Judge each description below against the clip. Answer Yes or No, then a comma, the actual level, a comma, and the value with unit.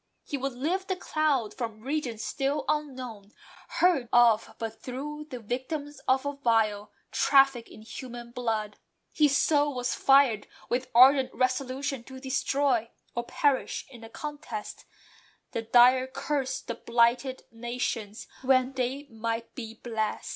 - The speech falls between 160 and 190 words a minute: No, average, 140 wpm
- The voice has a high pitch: Yes, very high, 255 Hz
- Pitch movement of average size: Yes, average, 3.2 semitones